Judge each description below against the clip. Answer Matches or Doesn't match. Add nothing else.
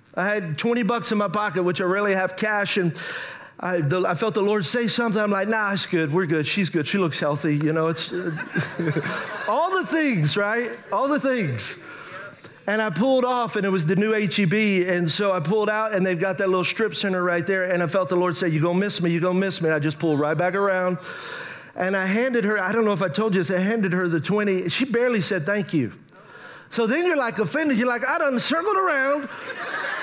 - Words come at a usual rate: Doesn't match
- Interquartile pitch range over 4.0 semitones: Doesn't match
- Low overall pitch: Doesn't match